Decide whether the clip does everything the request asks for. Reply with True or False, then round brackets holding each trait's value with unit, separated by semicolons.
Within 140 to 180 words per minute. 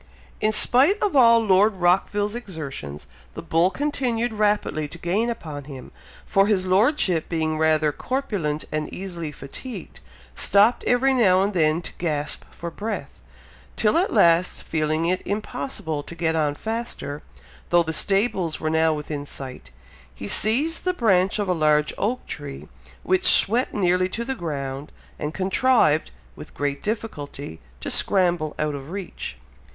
True (150 wpm)